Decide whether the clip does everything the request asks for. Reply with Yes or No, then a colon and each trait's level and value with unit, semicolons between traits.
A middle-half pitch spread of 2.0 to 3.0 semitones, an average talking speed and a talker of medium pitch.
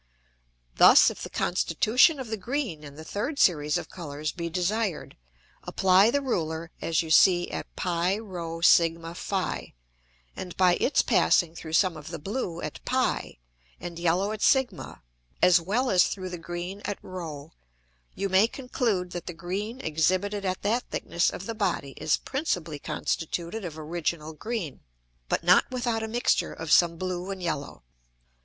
No: average, 3.8 semitones; average, 165 wpm; medium, 180 Hz